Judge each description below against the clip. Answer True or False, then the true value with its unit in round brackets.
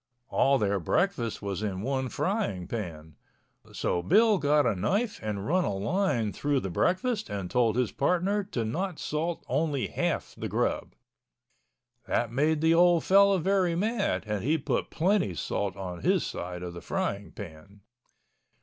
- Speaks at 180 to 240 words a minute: False (160 wpm)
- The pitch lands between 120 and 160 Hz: True (135 Hz)